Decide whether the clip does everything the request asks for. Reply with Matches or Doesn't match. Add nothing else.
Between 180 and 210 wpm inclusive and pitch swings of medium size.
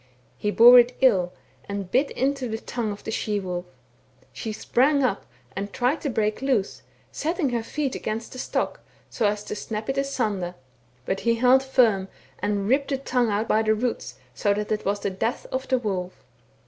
Matches